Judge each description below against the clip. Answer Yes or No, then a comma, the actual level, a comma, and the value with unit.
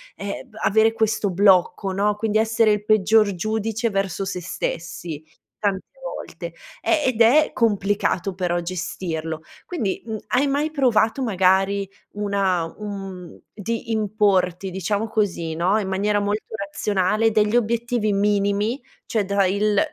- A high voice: Yes, high, 205 Hz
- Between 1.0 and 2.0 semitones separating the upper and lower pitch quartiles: No, narrow, 2.5 semitones